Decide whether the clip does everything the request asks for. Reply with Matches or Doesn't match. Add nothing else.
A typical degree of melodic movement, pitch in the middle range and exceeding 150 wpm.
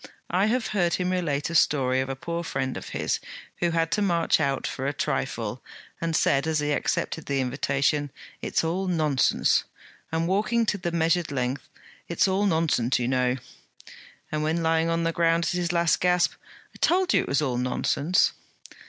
Matches